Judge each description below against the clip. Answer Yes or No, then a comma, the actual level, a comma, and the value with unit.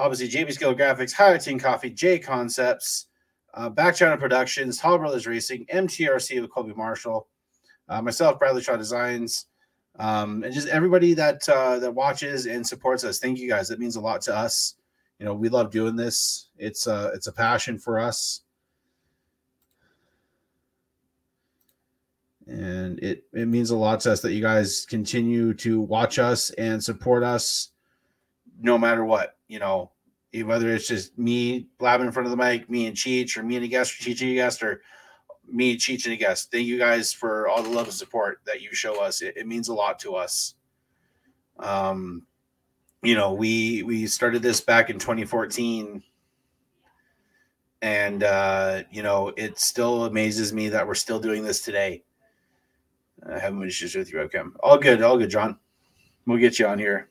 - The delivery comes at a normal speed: Yes, average, 180 wpm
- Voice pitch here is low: Yes, low, 120 Hz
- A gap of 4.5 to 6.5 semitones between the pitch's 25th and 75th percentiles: No, narrow, 2.6 semitones